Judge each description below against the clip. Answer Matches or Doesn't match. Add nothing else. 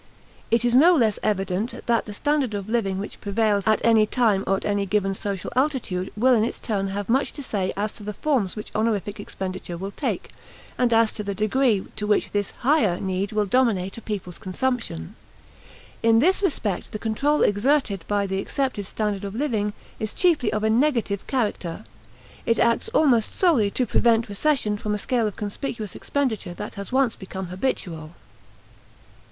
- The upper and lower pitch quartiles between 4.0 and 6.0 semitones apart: Doesn't match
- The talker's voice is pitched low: Doesn't match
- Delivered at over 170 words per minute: Matches